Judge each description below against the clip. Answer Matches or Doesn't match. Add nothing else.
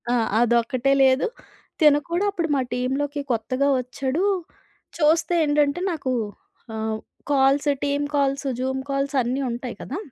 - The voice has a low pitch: Doesn't match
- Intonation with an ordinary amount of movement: Doesn't match